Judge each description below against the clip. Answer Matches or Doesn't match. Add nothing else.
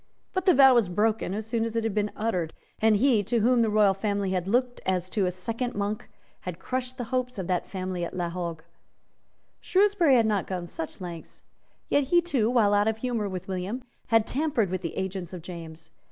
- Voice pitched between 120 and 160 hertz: Doesn't match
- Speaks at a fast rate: Matches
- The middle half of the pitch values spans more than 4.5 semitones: Matches